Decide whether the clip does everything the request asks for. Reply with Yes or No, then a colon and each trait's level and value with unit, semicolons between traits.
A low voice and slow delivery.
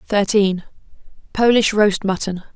No: high, 205 Hz; slow, 70 wpm